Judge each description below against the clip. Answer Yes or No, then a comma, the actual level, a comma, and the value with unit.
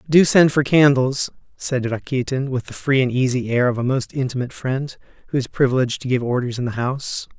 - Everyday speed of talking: No, fast, 210 wpm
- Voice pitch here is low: Yes, low, 130 Hz